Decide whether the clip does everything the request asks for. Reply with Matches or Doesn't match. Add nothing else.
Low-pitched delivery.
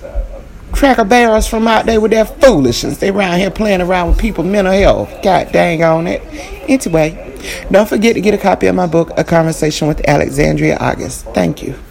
Doesn't match